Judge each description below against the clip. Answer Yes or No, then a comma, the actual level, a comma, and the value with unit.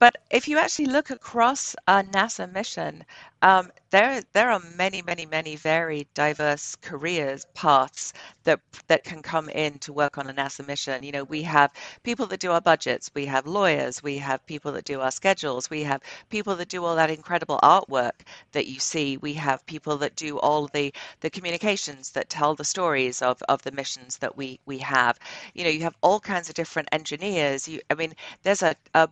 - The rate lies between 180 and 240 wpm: Yes, average, 200 wpm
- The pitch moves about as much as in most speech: Yes, average, 4.0 semitones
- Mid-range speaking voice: Yes, medium, 155 Hz